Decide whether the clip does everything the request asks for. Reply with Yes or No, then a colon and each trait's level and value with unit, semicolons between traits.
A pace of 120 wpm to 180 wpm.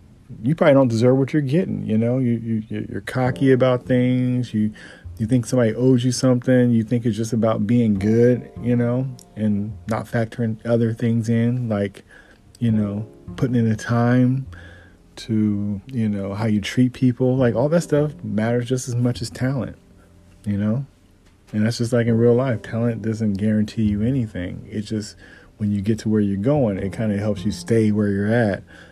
No: average, 195 wpm